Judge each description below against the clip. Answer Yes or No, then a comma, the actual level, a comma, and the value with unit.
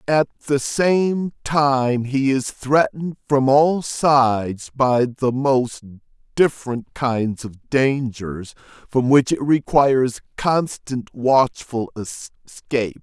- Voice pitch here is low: Yes, low, 130 Hz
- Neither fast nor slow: No, slow, 115 wpm